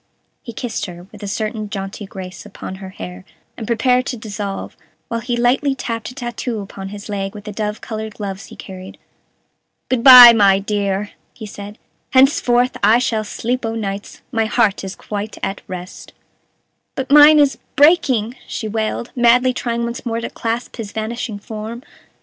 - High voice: Yes, high, 220 Hz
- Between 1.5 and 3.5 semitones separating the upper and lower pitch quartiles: Yes, average, 3.1 semitones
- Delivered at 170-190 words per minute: Yes, average, 175 wpm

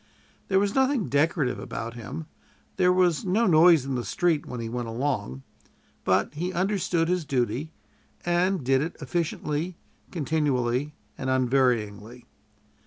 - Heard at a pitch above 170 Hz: No, medium, 150 Hz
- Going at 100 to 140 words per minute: Yes, slow, 135 wpm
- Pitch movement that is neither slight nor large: No, wide, 6.0 semitones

